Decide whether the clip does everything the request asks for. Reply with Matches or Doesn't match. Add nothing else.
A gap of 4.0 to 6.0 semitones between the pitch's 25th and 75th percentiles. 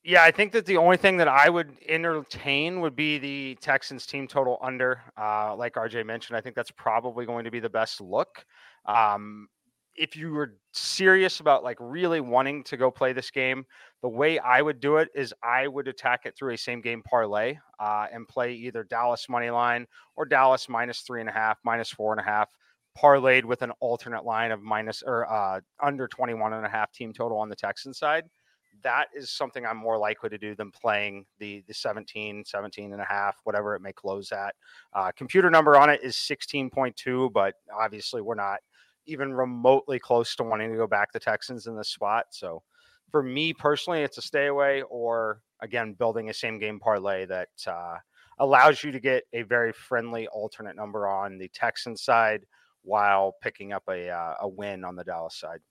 Matches